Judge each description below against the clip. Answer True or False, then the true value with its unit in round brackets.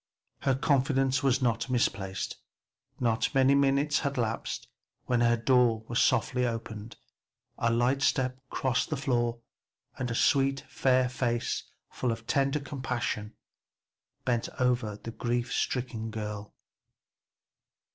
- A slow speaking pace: True (125 wpm)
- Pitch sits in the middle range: False (125 Hz)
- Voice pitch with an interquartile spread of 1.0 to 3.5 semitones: True (2.5 semitones)